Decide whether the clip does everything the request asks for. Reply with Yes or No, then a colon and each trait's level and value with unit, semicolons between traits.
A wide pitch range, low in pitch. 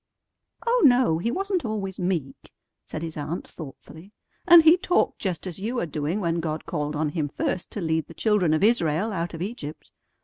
No: wide, 5.8 semitones; medium, 175 Hz